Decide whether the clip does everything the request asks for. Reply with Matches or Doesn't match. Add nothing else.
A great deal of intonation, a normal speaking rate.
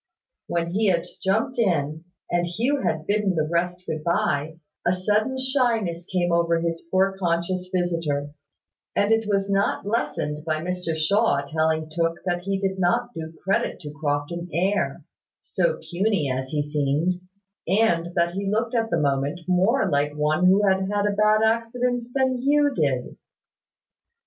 Doesn't match